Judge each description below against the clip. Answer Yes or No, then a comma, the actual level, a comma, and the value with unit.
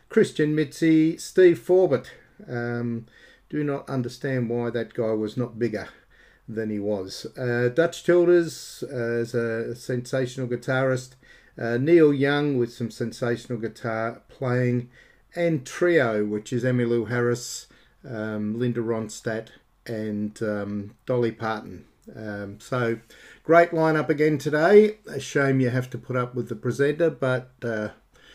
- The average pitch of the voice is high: No, low, 125 Hz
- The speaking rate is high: No, average, 140 wpm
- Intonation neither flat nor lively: Yes, average, 3.8 semitones